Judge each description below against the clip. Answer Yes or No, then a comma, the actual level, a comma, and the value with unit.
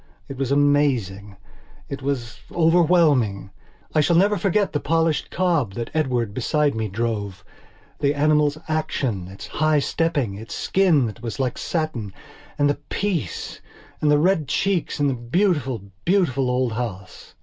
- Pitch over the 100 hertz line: Yes, medium, 140 Hz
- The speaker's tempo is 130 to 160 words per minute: Yes, average, 150 wpm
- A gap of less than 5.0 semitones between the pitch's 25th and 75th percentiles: No, average, 5.3 semitones